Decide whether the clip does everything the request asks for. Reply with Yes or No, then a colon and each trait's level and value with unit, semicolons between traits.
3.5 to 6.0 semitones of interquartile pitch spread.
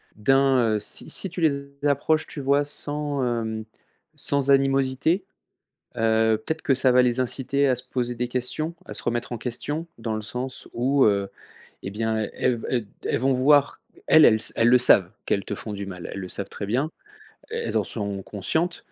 Yes: average, 4.0 semitones